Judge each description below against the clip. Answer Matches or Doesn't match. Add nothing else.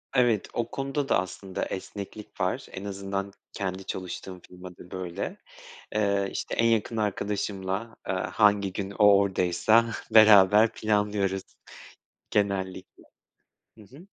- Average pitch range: Doesn't match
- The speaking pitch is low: Matches